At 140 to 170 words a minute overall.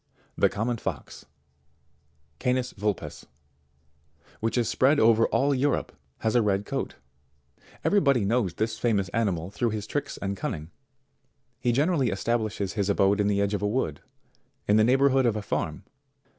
Yes: average, 165 wpm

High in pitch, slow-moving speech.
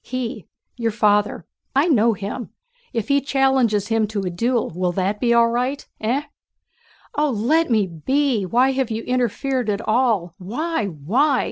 No: high, 230 Hz; average, 160 wpm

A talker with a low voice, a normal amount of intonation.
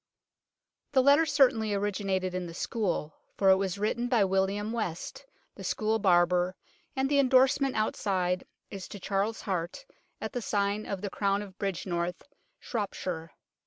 No: high, 200 Hz; average, 3.5 semitones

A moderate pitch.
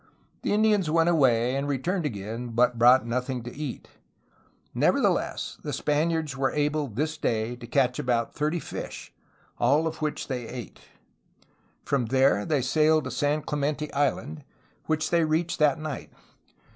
Yes: medium, 145 Hz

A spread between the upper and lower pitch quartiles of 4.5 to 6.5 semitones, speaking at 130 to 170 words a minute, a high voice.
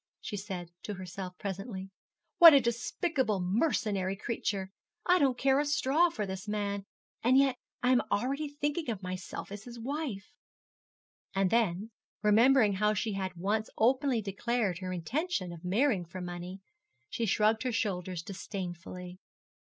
Yes: average, 5.2 semitones; average, 150 wpm; high, 210 Hz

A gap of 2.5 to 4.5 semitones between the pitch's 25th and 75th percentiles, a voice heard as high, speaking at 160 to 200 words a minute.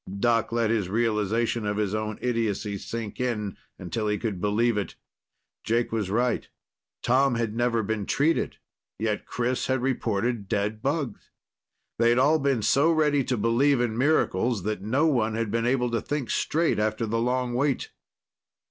No: average, 2.8 semitones; low, 115 Hz; average, 165 wpm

